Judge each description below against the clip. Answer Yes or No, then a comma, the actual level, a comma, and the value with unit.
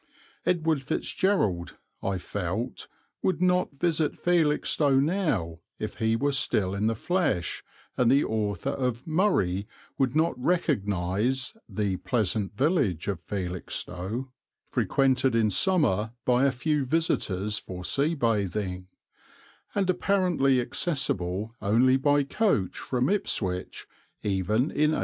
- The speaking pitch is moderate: No, low, 125 Hz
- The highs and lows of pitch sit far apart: Yes, wide, 7.3 semitones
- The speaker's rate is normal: No, slow, 120 wpm